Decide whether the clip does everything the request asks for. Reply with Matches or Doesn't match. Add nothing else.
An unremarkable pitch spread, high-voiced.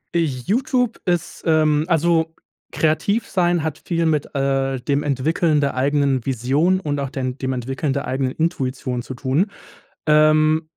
Doesn't match